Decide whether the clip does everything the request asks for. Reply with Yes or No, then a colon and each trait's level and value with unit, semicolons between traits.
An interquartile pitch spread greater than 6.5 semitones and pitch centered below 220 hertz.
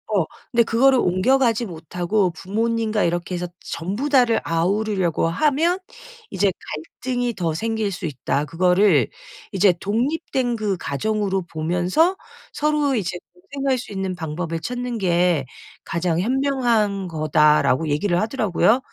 No: wide, 5.6 semitones; high, 195 Hz